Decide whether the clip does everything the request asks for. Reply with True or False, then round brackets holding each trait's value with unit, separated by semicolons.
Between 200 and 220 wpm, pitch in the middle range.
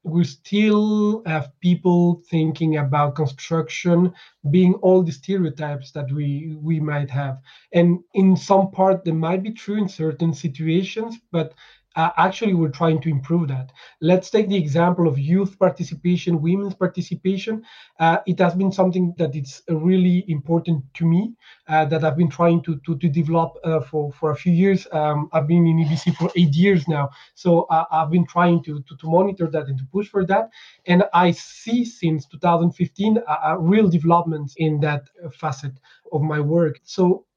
False (175 wpm; 170 Hz)